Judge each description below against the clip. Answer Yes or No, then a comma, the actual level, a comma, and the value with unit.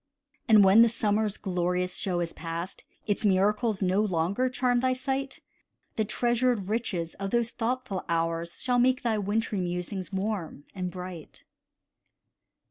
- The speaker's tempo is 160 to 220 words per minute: No, average, 140 wpm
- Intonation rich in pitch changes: No, average, 4.6 semitones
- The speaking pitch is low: No, high, 205 Hz